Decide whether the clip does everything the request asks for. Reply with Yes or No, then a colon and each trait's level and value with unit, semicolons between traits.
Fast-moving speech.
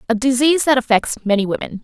No: average, 195 wpm